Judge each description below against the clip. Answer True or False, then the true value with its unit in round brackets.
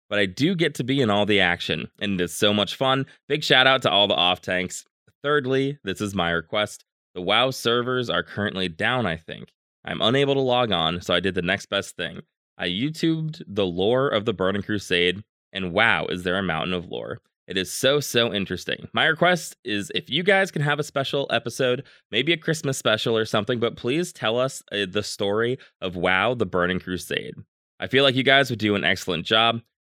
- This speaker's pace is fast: True (215 wpm)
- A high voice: False (110 Hz)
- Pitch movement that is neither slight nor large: False (6.1 semitones)